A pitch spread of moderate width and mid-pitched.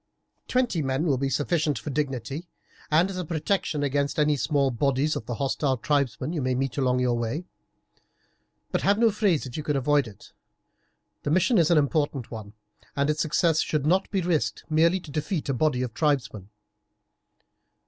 Yes: average, 3.5 semitones; medium, 145 Hz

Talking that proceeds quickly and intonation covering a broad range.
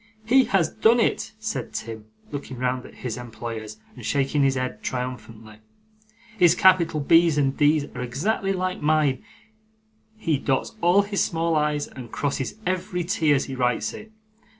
No: average, 160 wpm; wide, 5.7 semitones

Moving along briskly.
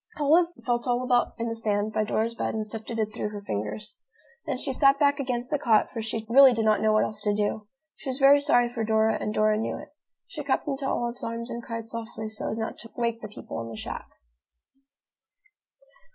Yes: fast, 225 wpm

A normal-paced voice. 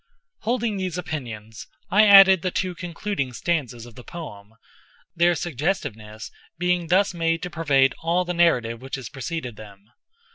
Yes: average, 145 wpm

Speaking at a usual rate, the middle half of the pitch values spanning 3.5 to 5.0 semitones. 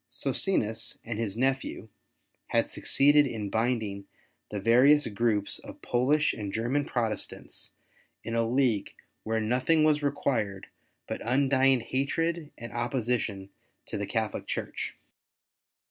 No: slow, 120 wpm; average, 3.9 semitones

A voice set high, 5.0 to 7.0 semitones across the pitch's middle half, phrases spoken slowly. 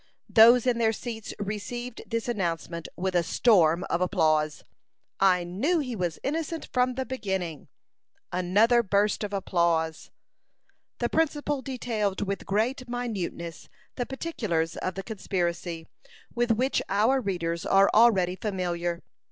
Yes: high, 205 Hz; wide, 5.5 semitones; slow, 130 wpm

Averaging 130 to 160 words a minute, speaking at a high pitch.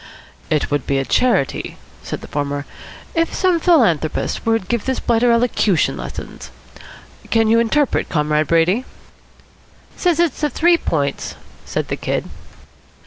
Yes: average, 140 wpm; high, 225 Hz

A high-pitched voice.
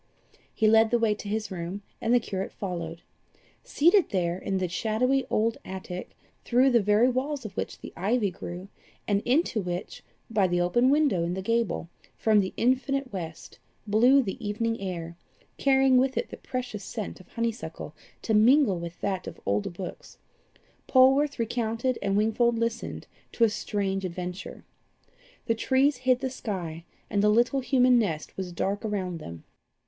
Yes: high, 215 Hz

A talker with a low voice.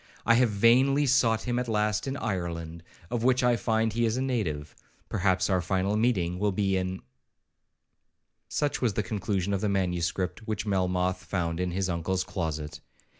Yes: low, 100 Hz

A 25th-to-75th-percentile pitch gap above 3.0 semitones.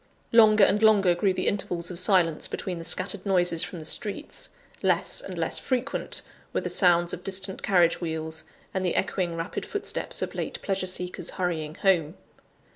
No: narrow, 2.5 semitones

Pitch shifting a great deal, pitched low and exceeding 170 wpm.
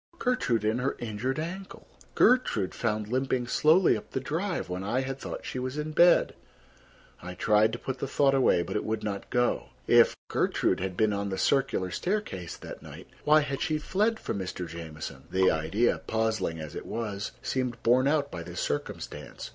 Yes: wide, 6.1 semitones; low, 120 Hz; average, 185 wpm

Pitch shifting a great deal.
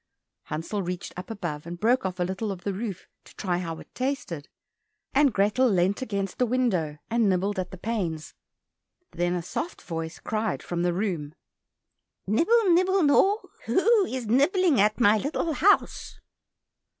Yes: wide, 6.6 semitones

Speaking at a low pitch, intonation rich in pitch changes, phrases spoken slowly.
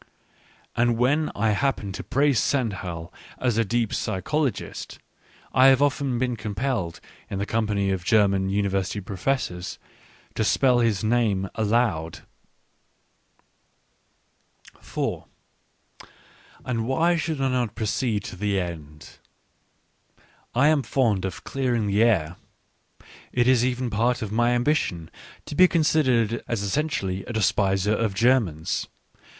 No: low, 115 Hz; average, 4.7 semitones; slow, 125 wpm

